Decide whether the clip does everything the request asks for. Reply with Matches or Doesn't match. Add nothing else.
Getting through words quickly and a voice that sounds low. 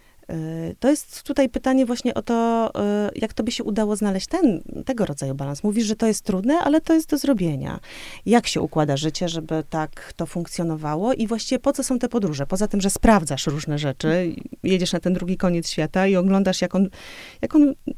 Doesn't match